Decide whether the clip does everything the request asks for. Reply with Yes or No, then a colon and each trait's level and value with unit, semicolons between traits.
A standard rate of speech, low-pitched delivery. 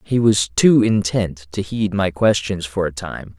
Yes: average, 195 wpm; very low, 95 Hz